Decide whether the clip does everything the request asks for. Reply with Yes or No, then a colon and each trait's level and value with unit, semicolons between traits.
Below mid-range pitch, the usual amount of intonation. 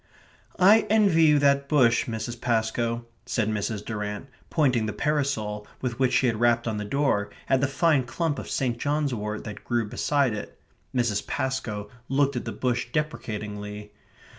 Yes: low, 120 Hz; average, 4.6 semitones